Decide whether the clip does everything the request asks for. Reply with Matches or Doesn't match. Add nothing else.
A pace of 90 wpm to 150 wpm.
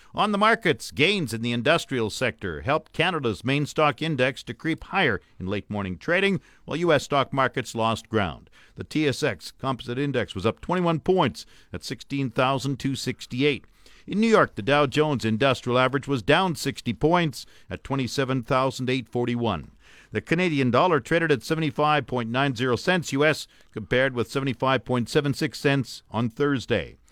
Matches